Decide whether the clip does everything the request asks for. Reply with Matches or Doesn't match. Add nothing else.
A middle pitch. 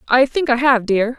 Doesn't match